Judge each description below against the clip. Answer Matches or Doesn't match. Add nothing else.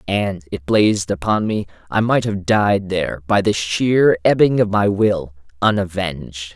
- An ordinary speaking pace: Matches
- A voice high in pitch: Doesn't match